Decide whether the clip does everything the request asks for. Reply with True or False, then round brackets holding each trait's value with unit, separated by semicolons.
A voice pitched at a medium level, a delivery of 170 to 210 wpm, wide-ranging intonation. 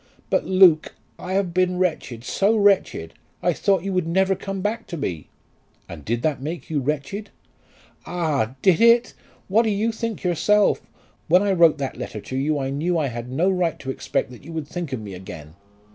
True (170 Hz; 200 wpm; 6.1 semitones)